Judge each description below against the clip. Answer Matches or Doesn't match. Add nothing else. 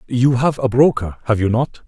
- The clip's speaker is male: Matches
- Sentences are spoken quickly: Matches